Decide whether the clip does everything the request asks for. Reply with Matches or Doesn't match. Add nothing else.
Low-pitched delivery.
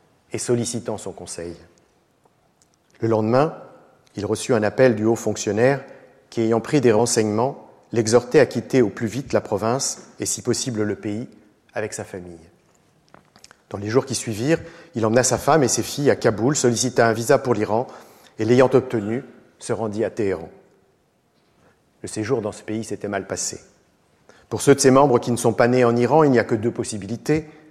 Matches